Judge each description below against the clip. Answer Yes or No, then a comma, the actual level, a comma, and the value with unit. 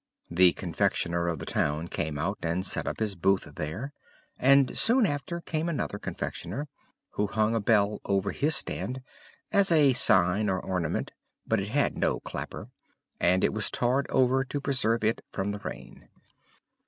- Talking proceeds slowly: No, average, 165 wpm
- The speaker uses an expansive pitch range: Yes, wide, 6.7 semitones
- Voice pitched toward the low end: Yes, low, 105 Hz